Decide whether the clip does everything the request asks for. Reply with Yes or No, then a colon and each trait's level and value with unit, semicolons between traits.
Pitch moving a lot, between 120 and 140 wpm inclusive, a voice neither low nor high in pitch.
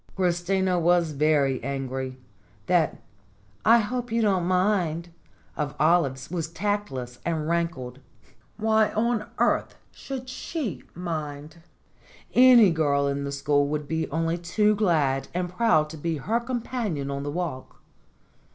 Yes: wide, 6.3 semitones; slow, 135 wpm; medium, 170 Hz